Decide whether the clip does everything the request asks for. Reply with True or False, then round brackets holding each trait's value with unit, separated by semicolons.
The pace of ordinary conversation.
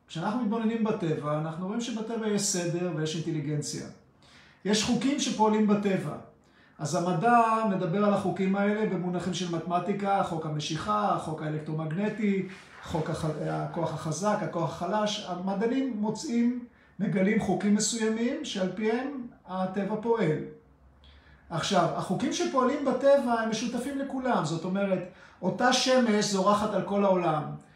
True (125 wpm)